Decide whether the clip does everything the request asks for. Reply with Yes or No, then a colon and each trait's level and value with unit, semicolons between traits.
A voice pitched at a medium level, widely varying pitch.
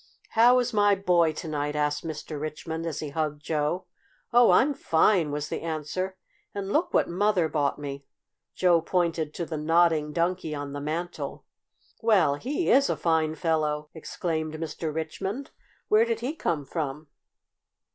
No: medium, 160 Hz; average, 3.8 semitones